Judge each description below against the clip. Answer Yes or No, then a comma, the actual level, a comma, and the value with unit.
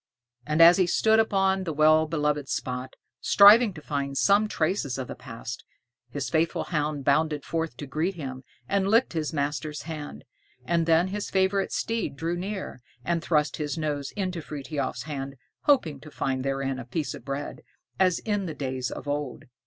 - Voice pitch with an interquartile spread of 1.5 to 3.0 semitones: No, average, 4.6 semitones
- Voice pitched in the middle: Yes, medium, 155 Hz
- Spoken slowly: No, average, 175 wpm